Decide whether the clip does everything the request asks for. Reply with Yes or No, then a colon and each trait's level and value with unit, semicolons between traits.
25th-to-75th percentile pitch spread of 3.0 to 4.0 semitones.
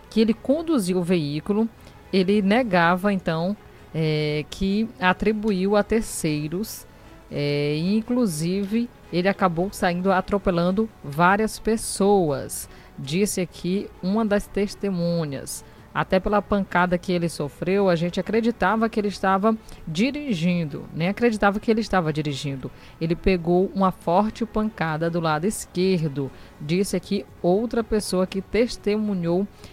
Yes: average, 3.5 semitones